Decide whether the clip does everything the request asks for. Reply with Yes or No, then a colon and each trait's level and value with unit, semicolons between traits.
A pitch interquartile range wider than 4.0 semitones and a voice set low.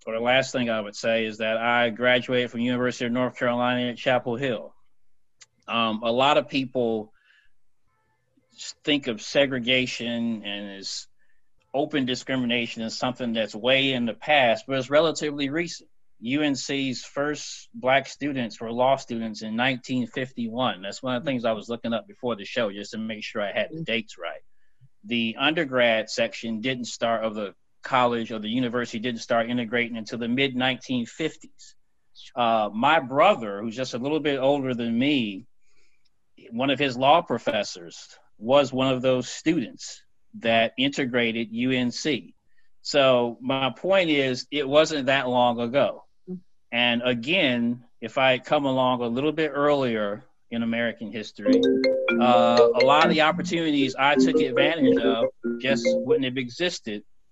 No: average, 2.7 semitones; low, 125 Hz